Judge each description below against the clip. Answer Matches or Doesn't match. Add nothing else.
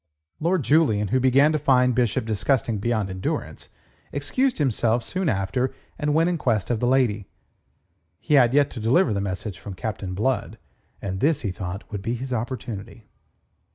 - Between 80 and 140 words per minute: Doesn't match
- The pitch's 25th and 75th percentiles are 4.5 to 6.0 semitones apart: Matches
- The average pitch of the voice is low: Matches